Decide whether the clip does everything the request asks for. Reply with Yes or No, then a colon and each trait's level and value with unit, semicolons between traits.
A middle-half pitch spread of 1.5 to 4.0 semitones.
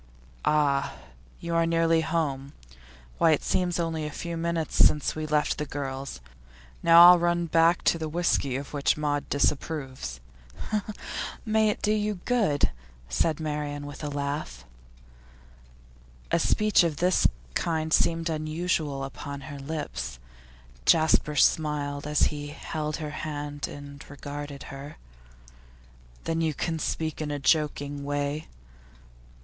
Yes: narrow, 2.4 semitones